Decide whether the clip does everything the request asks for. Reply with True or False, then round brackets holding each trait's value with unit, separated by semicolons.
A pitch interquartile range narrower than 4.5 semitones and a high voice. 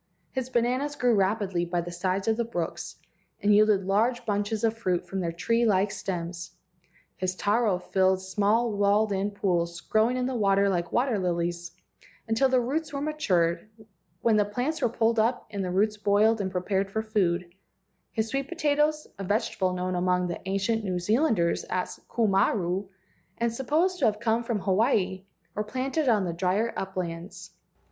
True (4.1 semitones; 205 Hz)